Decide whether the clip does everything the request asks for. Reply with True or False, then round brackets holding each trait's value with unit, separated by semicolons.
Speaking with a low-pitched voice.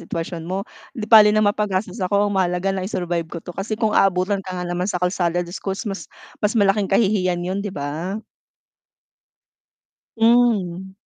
False (190 Hz)